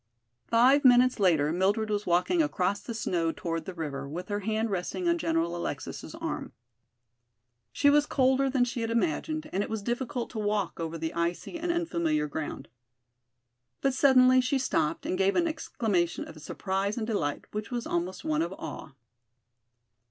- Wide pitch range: Yes, wide, 7.0 semitones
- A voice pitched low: No, high, 205 Hz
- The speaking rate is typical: Yes, average, 170 wpm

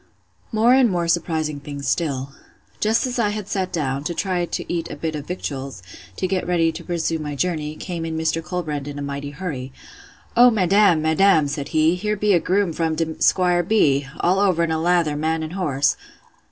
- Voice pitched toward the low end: No, medium, 165 Hz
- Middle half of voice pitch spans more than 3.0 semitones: Yes, average, 3.5 semitones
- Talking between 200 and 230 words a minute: Yes, fast, 205 wpm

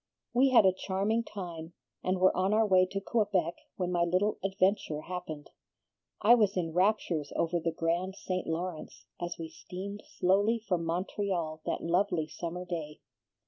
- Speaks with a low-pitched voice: No, medium, 185 Hz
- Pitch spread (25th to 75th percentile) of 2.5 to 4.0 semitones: Yes, average, 2.9 semitones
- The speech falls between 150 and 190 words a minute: Yes, average, 160 wpm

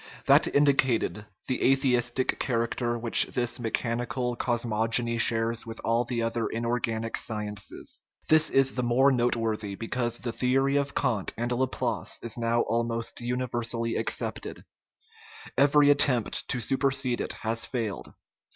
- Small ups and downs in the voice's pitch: Yes, narrow, 1.9 semitones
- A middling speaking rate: No, slow, 130 wpm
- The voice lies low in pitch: Yes, low, 120 Hz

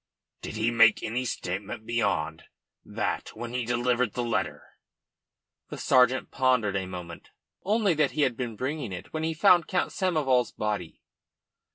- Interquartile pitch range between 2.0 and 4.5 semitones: No, average, 5.1 semitones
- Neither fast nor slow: Yes, average, 155 wpm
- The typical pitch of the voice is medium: No, low, 125 Hz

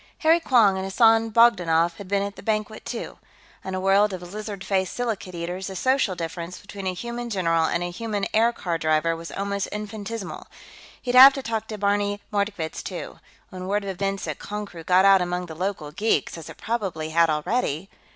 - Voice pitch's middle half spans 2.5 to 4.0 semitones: Yes, average, 3.5 semitones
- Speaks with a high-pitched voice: Yes, high, 195 Hz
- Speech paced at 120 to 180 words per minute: No, average, 195 wpm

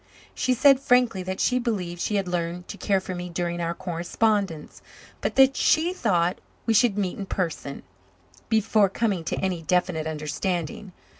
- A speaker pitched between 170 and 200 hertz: Yes, medium, 185 Hz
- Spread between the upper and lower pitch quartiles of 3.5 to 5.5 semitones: Yes, average, 4.2 semitones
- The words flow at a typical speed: Yes, average, 165 wpm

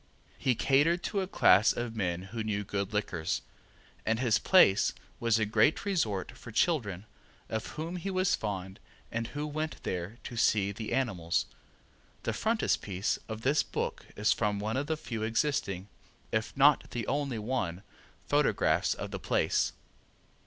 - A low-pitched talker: Yes, low, 110 Hz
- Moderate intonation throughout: No, wide, 6.2 semitones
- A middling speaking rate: Yes, average, 160 wpm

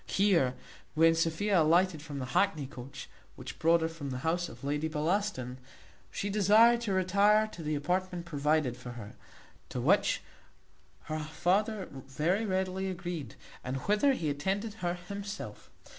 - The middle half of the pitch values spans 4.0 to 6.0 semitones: Yes, average, 5.1 semitones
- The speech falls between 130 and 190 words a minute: Yes, average, 150 wpm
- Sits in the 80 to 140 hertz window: No, medium, 170 Hz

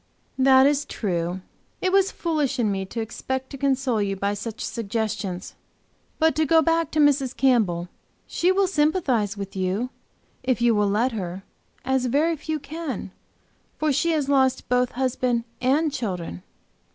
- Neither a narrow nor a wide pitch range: No, wide, 6.1 semitones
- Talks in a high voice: Yes, very high, 255 Hz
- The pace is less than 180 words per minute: Yes, average, 160 wpm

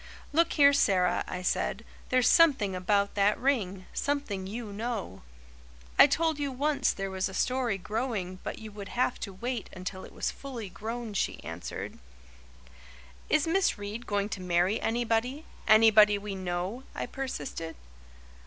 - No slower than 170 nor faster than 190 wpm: No, average, 155 wpm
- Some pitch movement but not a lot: Yes, average, 4.9 semitones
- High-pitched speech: Yes, high, 215 Hz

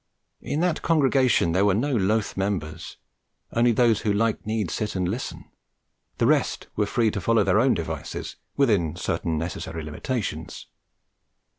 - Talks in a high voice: No, low, 105 Hz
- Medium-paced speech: Yes, average, 150 wpm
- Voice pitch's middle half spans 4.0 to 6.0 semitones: Yes, average, 4.4 semitones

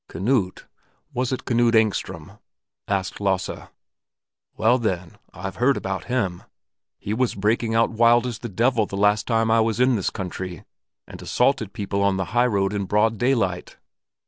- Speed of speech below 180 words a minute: Yes, average, 170 wpm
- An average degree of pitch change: Yes, average, 3.5 semitones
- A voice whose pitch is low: Yes, low, 110 Hz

